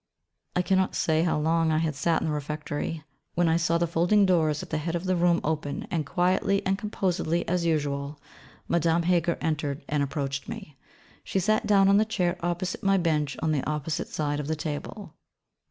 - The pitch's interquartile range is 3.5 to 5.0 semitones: No, average, 3.0 semitones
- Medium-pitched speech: Yes, medium, 165 Hz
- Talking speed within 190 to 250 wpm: Yes, average, 200 wpm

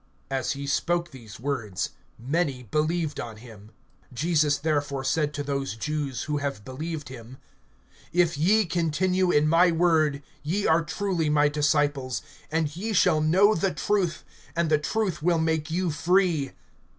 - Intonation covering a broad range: No, average, 3.4 semitones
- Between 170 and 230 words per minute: No, average, 150 wpm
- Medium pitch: Yes, medium, 155 Hz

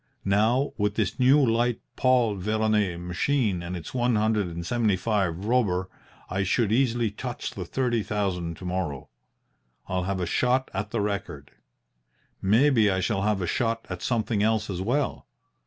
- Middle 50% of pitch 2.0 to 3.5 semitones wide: No, average, 4.2 semitones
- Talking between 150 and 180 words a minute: Yes, average, 165 wpm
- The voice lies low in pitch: Yes, low, 105 Hz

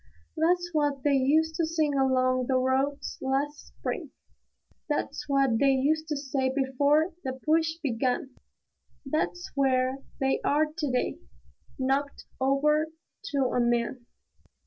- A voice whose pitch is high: Yes, very high, 275 Hz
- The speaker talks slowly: Yes, slow, 130 wpm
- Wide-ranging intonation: No, narrow, 2.5 semitones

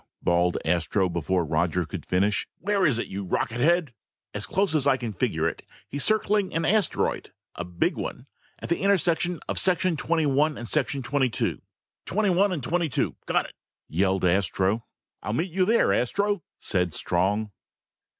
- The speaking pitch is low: Yes, low, 130 Hz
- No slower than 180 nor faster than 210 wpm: No, average, 170 wpm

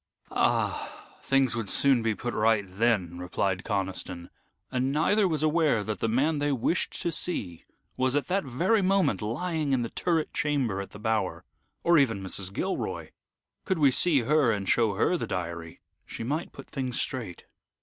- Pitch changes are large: Yes, wide, 6.8 semitones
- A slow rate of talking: No, average, 175 wpm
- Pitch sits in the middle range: No, low, 125 Hz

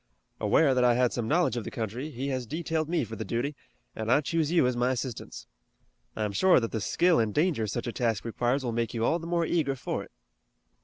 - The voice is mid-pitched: No, low, 125 Hz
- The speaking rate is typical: No, fast, 240 wpm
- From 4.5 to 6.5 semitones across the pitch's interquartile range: Yes, average, 5.2 semitones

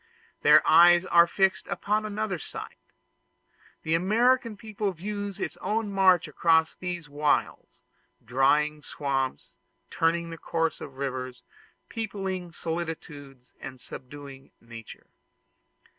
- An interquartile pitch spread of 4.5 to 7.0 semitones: Yes, average, 5.2 semitones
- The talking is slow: Yes, slow, 110 wpm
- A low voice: No, medium, 165 Hz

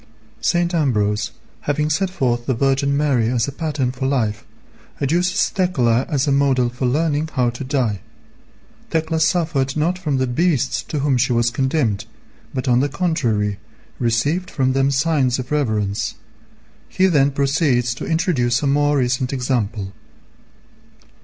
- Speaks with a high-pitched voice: No, low, 135 Hz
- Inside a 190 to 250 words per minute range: No, average, 150 wpm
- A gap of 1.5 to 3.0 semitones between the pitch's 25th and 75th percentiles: No, average, 3.8 semitones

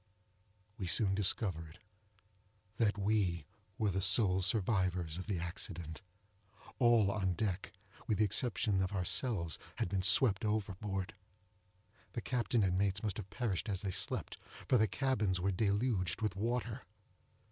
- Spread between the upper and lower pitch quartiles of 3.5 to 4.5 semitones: No, average, 2.8 semitones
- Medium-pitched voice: No, low, 100 Hz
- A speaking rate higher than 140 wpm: No, slow, 135 wpm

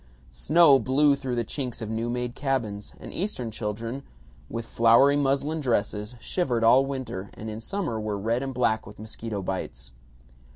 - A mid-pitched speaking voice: No, low, 115 Hz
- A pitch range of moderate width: Yes, average, 4.0 semitones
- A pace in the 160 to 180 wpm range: Yes, average, 165 wpm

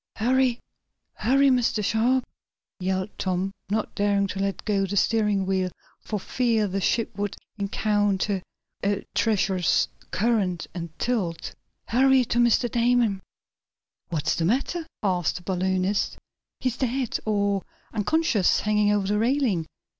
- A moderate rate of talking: No, slow, 130 wpm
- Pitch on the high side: Yes, high, 205 Hz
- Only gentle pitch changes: No, average, 3.8 semitones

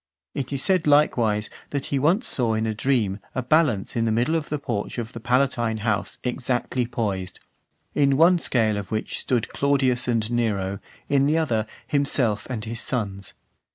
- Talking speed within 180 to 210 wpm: Yes, average, 185 wpm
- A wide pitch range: No, average, 4.2 semitones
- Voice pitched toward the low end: Yes, low, 120 Hz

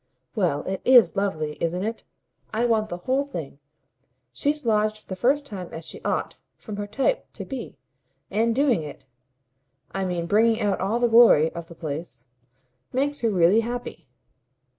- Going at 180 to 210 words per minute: No, average, 170 wpm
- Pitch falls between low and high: No, high, 210 Hz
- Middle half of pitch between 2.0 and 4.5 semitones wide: No, wide, 5.6 semitones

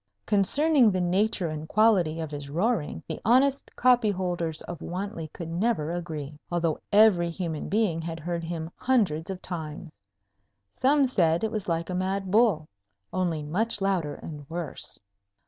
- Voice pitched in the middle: Yes, medium, 175 Hz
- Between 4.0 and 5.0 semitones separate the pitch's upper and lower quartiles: Yes, average, 4.7 semitones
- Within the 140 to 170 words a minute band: Yes, average, 150 wpm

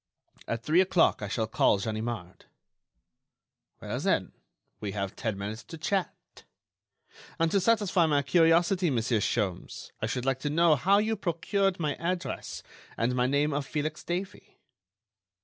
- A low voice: No, medium, 150 Hz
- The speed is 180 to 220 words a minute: No, average, 150 wpm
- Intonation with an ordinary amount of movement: No, wide, 7.3 semitones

